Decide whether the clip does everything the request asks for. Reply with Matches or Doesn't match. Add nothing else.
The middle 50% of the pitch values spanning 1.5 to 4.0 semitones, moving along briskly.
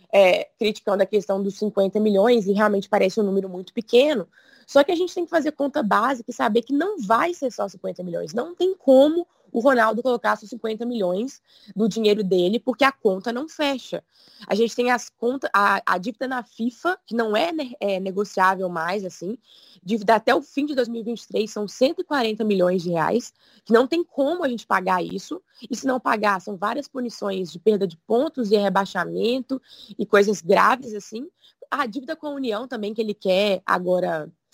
Doesn't match